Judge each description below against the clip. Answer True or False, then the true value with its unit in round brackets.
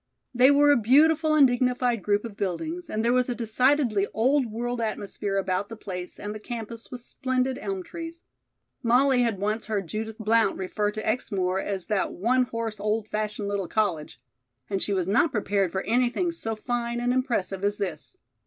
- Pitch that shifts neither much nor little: True (3.6 semitones)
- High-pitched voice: True (225 Hz)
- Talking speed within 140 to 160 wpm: False (185 wpm)